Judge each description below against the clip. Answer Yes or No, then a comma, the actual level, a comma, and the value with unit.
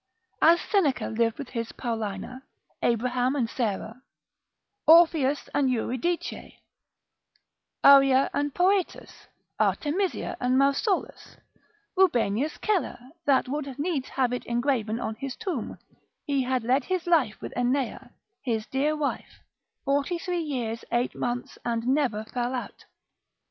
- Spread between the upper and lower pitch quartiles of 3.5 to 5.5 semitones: Yes, average, 3.9 semitones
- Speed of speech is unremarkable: No, slow, 125 wpm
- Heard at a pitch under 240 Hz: No, very high, 265 Hz